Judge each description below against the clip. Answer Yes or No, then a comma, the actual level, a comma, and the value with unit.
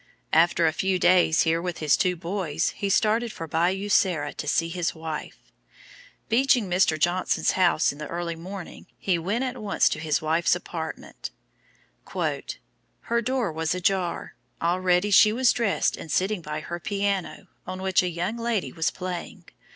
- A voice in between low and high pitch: Yes, medium, 180 Hz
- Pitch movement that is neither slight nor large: Yes, average, 3.3 semitones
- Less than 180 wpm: Yes, average, 165 wpm